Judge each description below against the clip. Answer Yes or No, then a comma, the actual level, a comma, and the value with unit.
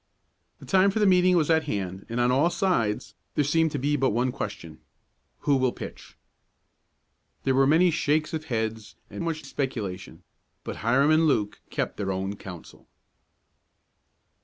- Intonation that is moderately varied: No, wide, 6.8 semitones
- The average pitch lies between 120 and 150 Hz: Yes, low, 135 Hz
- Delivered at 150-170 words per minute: Yes, average, 160 wpm